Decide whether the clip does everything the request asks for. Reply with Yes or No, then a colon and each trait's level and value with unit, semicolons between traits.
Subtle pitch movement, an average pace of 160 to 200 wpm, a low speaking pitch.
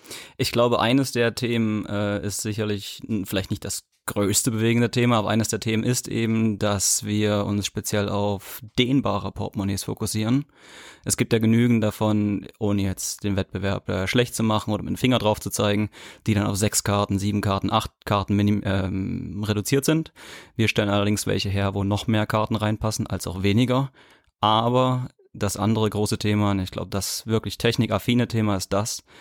Yes: narrow, 2.1 semitones; average, 185 wpm; low, 105 Hz